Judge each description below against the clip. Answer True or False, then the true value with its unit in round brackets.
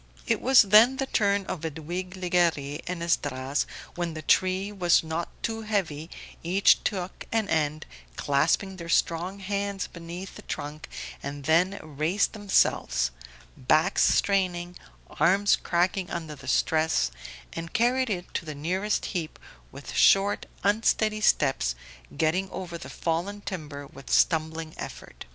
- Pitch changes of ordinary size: True (4.0 semitones)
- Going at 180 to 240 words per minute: False (135 wpm)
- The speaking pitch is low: False (175 Hz)